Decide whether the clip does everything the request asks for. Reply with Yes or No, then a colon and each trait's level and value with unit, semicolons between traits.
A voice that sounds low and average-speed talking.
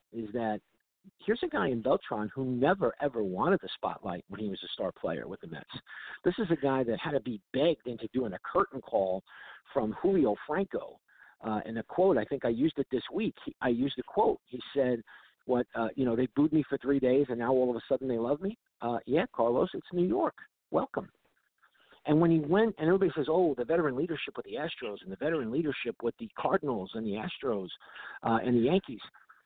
No: low, 130 Hz; fast, 225 wpm